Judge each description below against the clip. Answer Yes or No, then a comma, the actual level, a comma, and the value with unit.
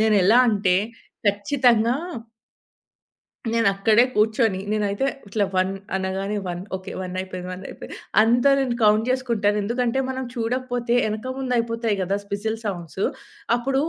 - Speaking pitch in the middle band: No, high, 220 Hz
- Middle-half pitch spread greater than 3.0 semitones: Yes, average, 3.4 semitones